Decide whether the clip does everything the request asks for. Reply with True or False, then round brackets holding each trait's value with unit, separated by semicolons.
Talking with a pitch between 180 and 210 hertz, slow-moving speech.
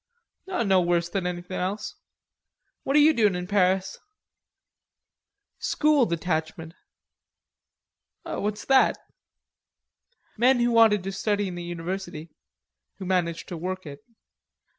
True (185 Hz; 115 wpm)